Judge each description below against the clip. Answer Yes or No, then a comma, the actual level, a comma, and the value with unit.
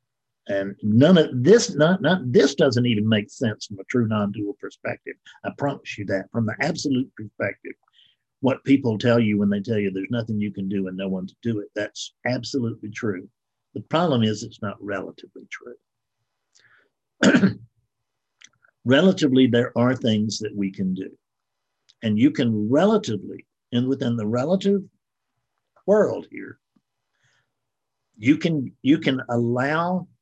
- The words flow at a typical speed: Yes, average, 150 wpm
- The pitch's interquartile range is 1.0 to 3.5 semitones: No, average, 4.5 semitones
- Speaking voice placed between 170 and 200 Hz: No, low, 115 Hz